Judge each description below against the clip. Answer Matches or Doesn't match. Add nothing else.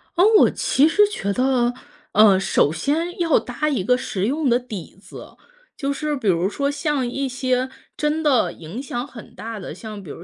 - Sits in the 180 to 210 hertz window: Doesn't match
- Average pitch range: Doesn't match